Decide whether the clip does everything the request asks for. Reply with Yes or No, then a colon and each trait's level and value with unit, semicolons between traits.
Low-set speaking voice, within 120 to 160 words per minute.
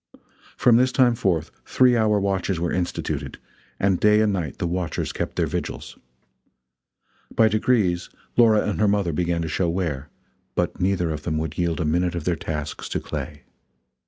No: very low, 90 Hz; average, 175 wpm